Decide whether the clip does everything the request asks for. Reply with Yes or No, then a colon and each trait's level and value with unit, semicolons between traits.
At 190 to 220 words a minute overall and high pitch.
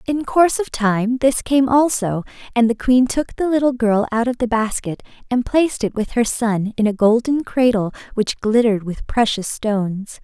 Yes: average, 195 wpm; high, 235 Hz